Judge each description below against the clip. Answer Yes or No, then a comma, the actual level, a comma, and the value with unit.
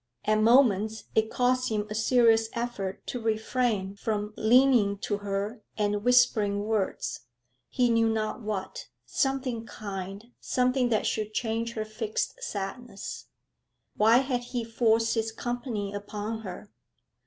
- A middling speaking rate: No, slow, 130 wpm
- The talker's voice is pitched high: Yes, high, 220 Hz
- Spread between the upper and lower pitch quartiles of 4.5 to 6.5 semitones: No, average, 2.7 semitones